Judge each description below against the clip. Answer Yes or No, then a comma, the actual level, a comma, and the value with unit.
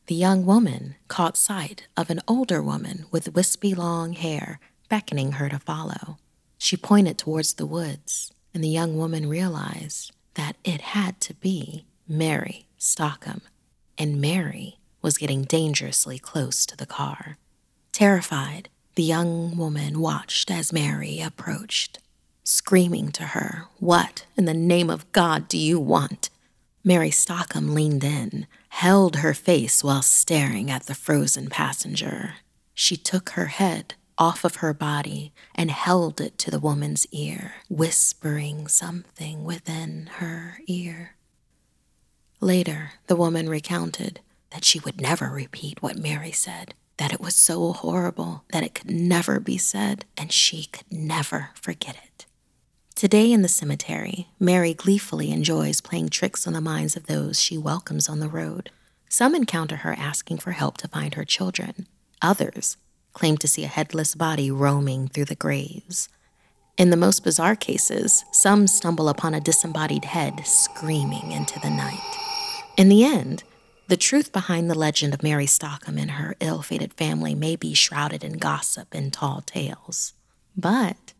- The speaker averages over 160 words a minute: No, average, 150 wpm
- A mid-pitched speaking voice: Yes, medium, 160 Hz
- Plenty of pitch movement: No, average, 4.0 semitones